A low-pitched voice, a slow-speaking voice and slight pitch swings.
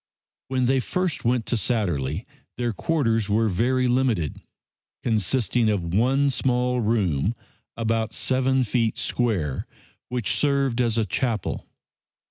No: low, 115 Hz; slow, 120 wpm; average, 3.3 semitones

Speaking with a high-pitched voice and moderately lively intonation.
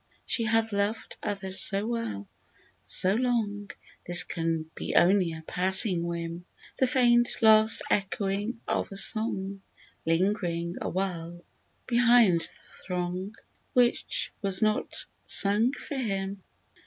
Yes: high, 195 Hz; average, 4.0 semitones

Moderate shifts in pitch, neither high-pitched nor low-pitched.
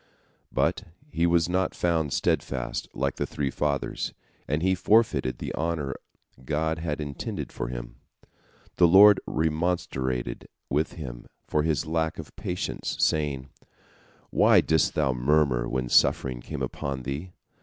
No: average, 3.8 semitones; very low, 75 Hz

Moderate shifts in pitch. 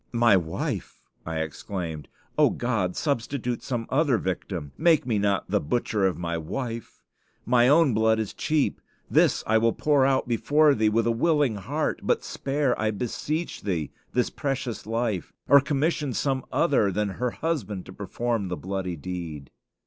No: wide, 6.1 semitones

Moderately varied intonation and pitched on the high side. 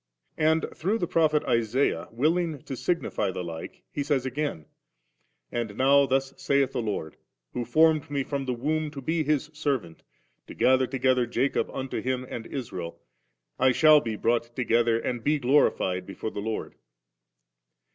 No: average, 4.2 semitones; low, 130 Hz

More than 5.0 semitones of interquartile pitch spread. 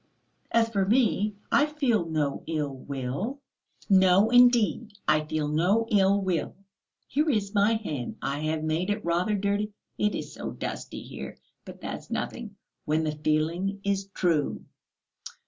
Yes: wide, 5.4 semitones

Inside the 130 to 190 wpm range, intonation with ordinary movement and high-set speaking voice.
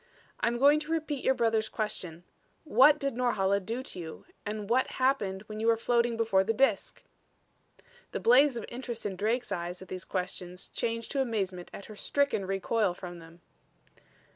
Yes: average, 175 wpm; average, 4.8 semitones; high, 225 Hz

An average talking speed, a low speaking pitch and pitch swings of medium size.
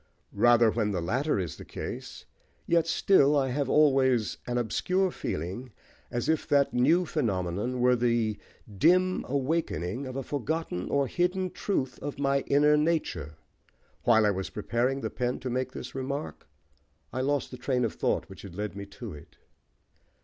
Yes: average, 165 wpm; low, 130 Hz; average, 4.7 semitones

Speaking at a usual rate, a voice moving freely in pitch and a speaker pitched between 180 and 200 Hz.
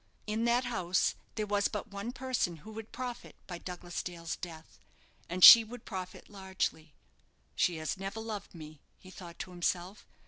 No: average, 170 wpm; average, 4.0 semitones; high, 190 Hz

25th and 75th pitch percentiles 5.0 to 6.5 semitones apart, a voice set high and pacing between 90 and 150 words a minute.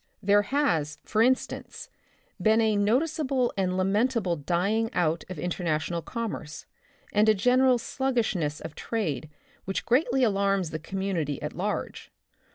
Yes: wide, 5.5 semitones; high, 200 Hz; slow, 135 wpm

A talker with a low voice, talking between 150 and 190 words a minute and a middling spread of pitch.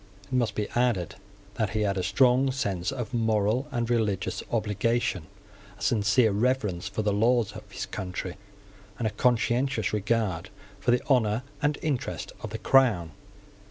Yes: low, 110 Hz; average, 160 wpm; average, 3.4 semitones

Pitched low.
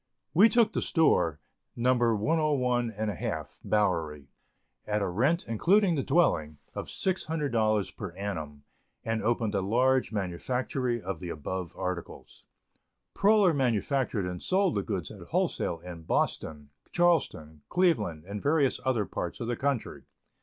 Yes: low, 115 Hz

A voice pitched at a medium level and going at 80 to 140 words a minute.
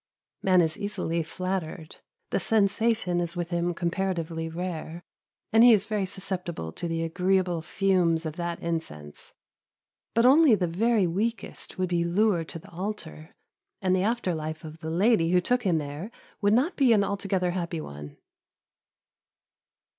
No: medium, 180 Hz; average, 155 wpm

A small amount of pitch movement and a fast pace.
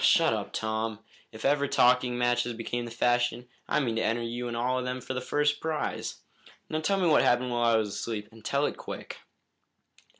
Yes: narrow, 1.8 semitones; fast, 210 wpm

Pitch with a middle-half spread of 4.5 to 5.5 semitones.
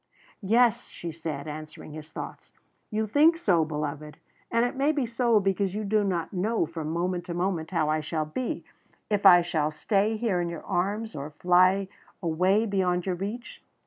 Yes: average, 4.9 semitones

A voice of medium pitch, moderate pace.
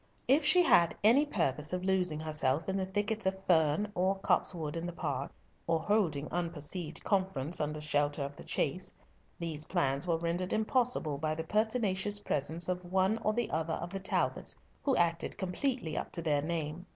Yes: medium, 175 Hz; average, 175 wpm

